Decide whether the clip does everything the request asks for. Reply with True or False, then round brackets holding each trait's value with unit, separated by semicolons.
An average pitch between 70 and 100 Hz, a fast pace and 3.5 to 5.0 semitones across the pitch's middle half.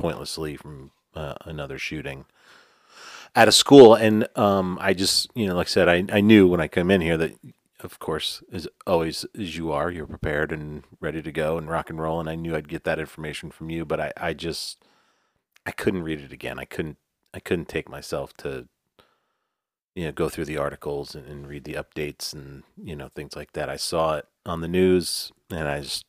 True (85 Hz; 215 wpm; 4.2 semitones)